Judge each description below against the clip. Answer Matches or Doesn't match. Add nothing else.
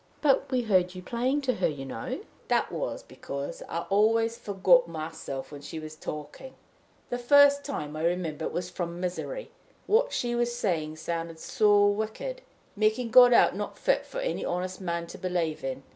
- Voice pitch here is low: Doesn't match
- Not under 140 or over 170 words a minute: Doesn't match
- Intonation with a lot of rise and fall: Matches